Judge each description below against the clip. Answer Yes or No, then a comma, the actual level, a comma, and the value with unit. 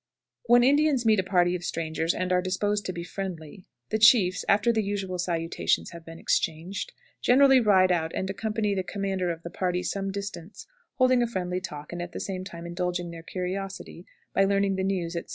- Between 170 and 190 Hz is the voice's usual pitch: Yes, medium, 185 Hz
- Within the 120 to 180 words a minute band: No, average, 200 wpm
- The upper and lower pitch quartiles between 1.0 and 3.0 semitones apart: Yes, narrow, 2.6 semitones